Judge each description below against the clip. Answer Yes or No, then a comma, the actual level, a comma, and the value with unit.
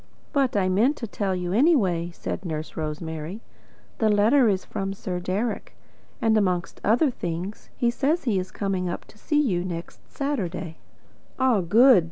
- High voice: Yes, high, 195 Hz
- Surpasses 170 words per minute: No, average, 165 wpm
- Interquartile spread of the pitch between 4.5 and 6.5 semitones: Yes, average, 5.2 semitones